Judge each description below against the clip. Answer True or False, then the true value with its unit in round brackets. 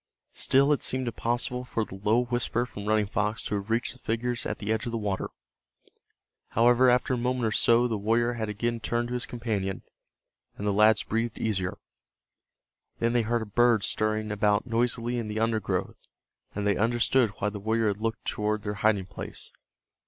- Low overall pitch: True (115 Hz)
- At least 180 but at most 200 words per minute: True (190 wpm)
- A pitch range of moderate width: False (2.3 semitones)